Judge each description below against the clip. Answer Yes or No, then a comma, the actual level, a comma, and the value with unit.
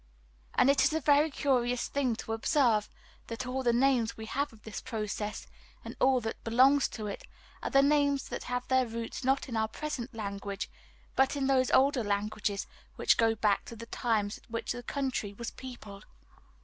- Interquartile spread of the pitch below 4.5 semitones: Yes, average, 3.5 semitones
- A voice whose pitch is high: Yes, high, 240 Hz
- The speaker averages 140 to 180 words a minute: No, average, 190 wpm